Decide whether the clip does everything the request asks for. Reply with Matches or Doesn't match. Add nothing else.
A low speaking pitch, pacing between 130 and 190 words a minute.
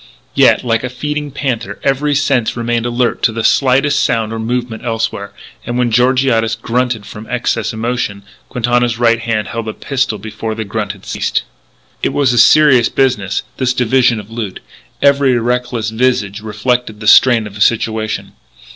Matches